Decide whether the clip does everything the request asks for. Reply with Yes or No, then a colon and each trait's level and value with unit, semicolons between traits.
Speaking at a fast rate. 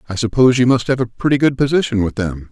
Yes: fast, 260 wpm